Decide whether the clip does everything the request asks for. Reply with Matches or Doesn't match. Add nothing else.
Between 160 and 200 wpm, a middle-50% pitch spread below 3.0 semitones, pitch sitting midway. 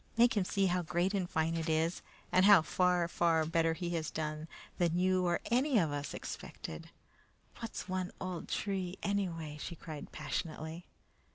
Matches